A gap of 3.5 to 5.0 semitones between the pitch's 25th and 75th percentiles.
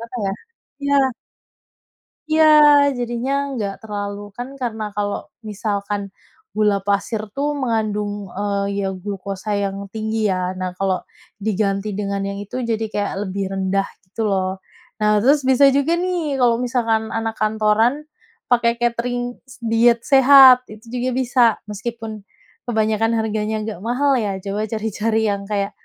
No: average, 2.9 semitones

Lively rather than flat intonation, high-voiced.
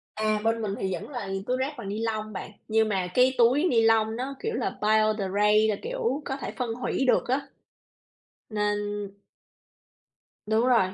No: average, 3.3 semitones; high, 225 Hz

